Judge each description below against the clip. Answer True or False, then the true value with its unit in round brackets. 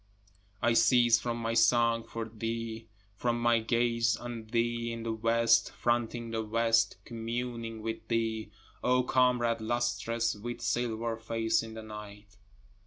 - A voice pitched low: True (115 Hz)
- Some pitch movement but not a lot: False (0.9 semitones)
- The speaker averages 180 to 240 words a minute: False (140 wpm)